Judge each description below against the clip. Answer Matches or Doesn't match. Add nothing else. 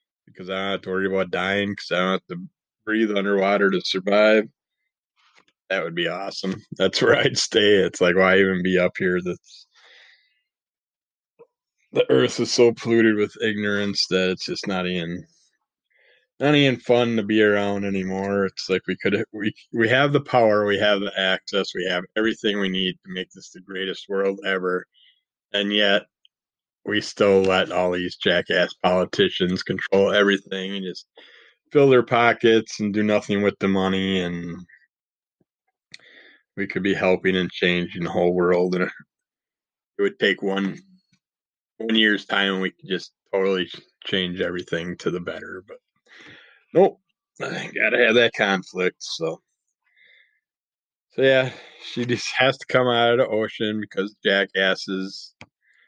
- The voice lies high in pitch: Doesn't match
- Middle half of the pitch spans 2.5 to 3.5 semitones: Matches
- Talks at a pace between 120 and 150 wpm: Doesn't match